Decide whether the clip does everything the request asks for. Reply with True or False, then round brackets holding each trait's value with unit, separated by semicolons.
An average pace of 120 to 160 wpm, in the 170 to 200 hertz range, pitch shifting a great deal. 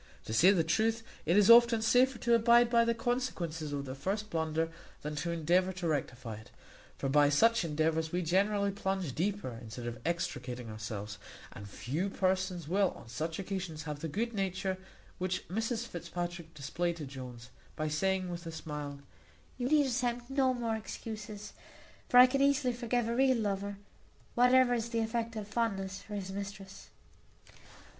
False (170 wpm; 190 Hz; 6.5 semitones)